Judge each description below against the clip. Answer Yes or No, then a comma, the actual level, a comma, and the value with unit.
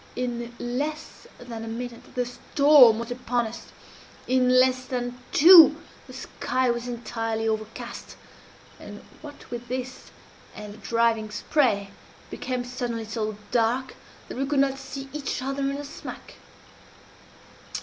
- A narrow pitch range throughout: Yes, narrow, 2.2 semitones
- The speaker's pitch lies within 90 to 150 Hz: No, high, 245 Hz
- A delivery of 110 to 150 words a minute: Yes, average, 140 wpm